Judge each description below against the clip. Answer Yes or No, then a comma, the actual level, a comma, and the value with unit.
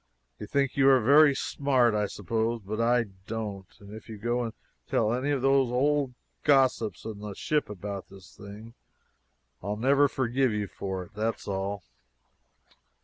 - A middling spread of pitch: Yes, average, 4.4 semitones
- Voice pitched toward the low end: Yes, low, 115 Hz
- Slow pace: No, average, 165 wpm